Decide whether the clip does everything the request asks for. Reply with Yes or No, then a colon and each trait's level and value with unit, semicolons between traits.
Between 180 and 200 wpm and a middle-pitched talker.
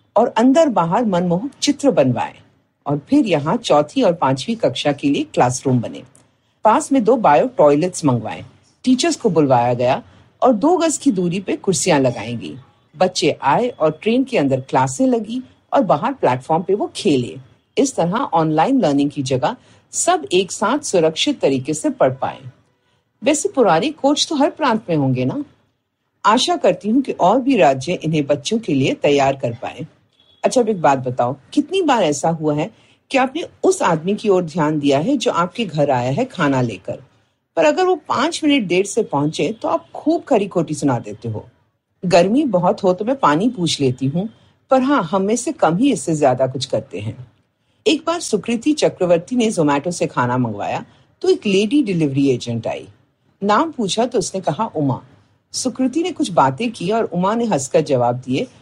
No: average, 155 wpm; medium, 175 Hz